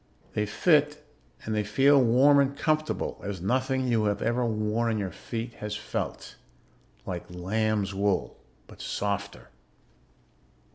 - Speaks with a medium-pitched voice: No, low, 110 Hz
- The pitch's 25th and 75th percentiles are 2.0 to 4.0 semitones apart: No, average, 4.4 semitones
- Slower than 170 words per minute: Yes, slow, 135 wpm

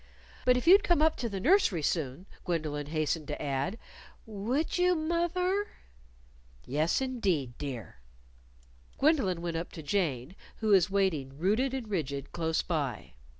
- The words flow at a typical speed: Yes, average, 150 wpm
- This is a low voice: No, medium, 185 Hz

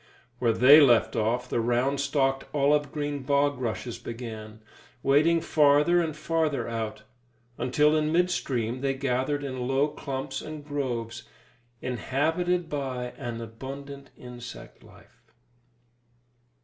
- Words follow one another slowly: Yes, slow, 120 wpm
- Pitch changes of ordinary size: Yes, average, 3.1 semitones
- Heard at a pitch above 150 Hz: No, low, 135 Hz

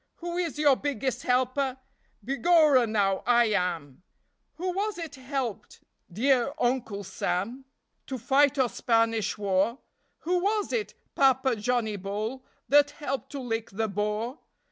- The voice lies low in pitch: No, very high, 255 Hz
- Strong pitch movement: No, average, 4.7 semitones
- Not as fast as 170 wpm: Yes, slow, 135 wpm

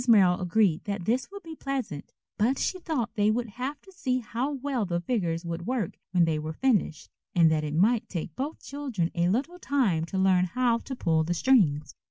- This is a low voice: No, high, 210 Hz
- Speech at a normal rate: No, fast, 210 wpm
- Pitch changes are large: Yes, wide, 7.3 semitones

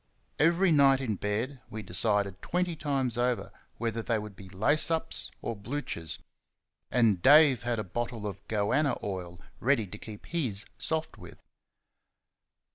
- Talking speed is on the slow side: No, average, 145 wpm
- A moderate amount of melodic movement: No, wide, 5.7 semitones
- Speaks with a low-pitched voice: Yes, low, 115 Hz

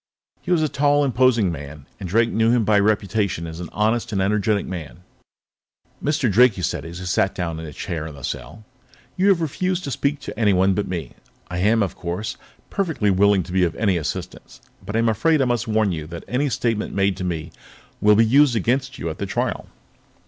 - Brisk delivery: Yes, fast, 215 wpm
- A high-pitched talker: No, low, 105 Hz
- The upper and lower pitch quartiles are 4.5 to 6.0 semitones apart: Yes, wide, 5.4 semitones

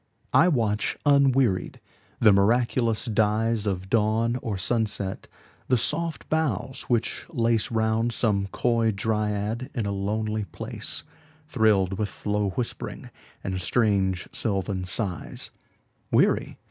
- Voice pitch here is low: Yes, low, 110 Hz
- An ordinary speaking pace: No, slow, 100 wpm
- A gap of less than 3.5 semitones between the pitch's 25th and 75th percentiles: Yes, average, 2.9 semitones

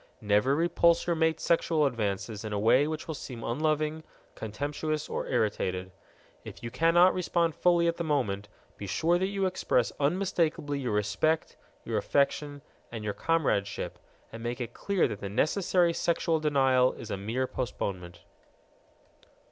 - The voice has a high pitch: No, medium, 145 Hz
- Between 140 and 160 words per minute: Yes, average, 155 wpm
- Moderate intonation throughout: No, wide, 7.0 semitones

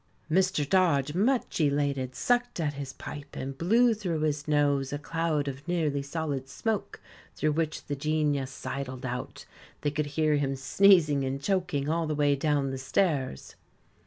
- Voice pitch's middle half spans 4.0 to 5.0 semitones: No, average, 3.1 semitones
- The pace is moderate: Yes, average, 160 wpm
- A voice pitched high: No, medium, 145 Hz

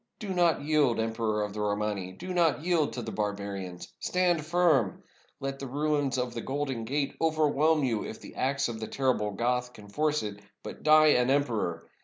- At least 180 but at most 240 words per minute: Yes, average, 200 wpm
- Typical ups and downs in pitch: No, wide, 6.0 semitones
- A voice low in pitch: Yes, low, 130 Hz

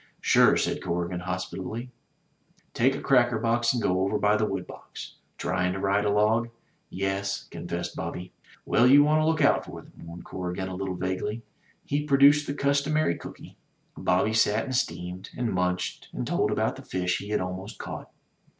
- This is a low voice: Yes, low, 100 Hz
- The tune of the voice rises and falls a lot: No, average, 5.0 semitones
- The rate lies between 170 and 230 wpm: Yes, average, 185 wpm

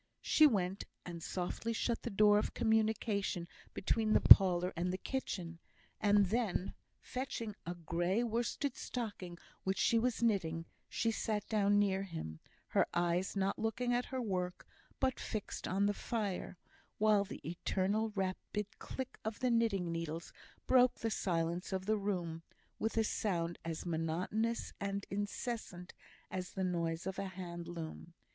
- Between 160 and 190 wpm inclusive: No, average, 150 wpm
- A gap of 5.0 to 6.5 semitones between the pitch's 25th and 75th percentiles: No, average, 4.0 semitones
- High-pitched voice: Yes, high, 195 Hz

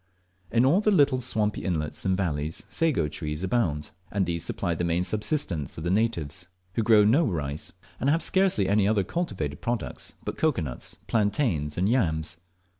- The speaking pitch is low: Yes, very low, 95 Hz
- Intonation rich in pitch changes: Yes, wide, 6.9 semitones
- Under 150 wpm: No, average, 175 wpm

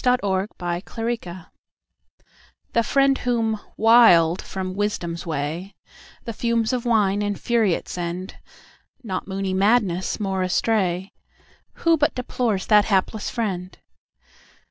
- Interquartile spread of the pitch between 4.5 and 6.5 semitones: No, average, 3.8 semitones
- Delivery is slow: Yes, slow, 95 wpm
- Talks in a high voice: Yes, high, 200 Hz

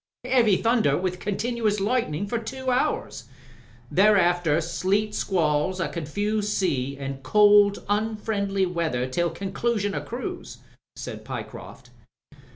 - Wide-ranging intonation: No, average, 4.2 semitones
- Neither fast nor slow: No, slow, 115 wpm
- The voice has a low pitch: No, high, 200 Hz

